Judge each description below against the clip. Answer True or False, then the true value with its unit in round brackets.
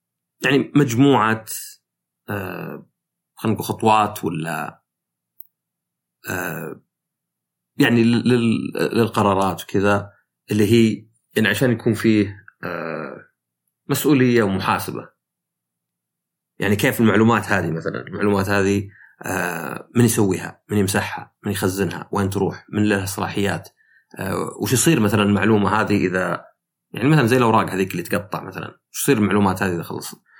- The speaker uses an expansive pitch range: False (3.2 semitones)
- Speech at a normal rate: True (105 wpm)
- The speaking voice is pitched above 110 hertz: False (105 Hz)